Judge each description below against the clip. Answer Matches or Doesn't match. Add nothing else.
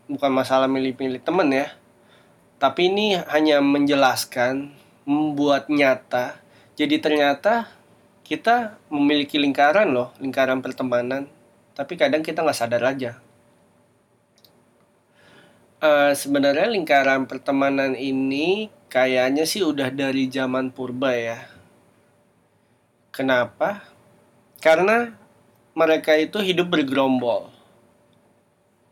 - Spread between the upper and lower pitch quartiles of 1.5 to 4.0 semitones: Matches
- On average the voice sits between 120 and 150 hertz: Matches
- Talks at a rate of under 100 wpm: Matches